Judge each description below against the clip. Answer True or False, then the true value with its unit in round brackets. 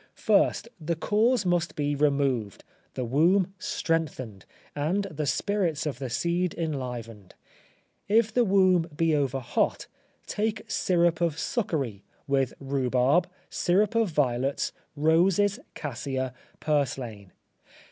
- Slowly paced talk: True (115 wpm)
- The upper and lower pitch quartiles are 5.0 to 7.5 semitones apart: True (5.6 semitones)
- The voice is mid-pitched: True (155 Hz)